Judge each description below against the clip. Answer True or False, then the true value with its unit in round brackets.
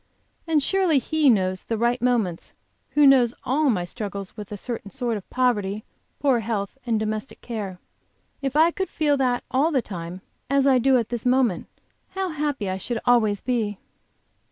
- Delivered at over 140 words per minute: True (180 wpm)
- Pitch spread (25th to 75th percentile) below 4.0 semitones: False (4.7 semitones)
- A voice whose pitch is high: True (240 Hz)